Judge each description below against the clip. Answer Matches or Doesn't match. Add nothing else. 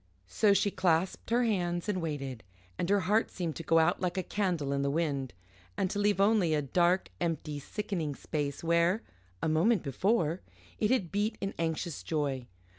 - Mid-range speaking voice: Matches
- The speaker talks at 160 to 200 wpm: Matches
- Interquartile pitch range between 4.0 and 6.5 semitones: Matches